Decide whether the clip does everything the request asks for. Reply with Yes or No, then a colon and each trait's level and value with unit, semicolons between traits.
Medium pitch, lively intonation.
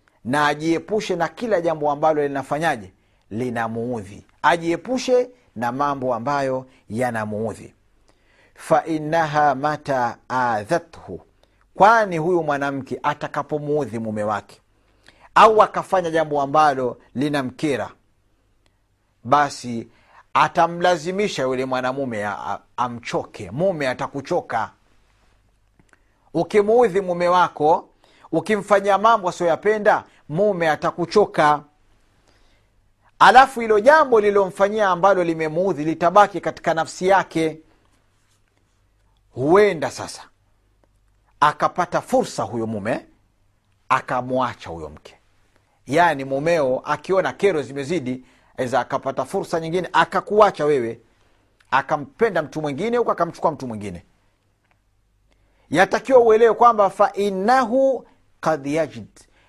Yes: medium, 145 Hz; wide, 8.6 semitones